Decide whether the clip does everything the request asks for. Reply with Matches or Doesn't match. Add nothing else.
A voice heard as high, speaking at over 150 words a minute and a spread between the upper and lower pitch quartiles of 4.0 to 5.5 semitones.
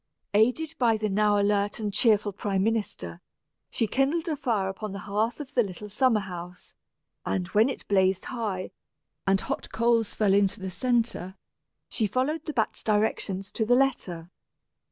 Doesn't match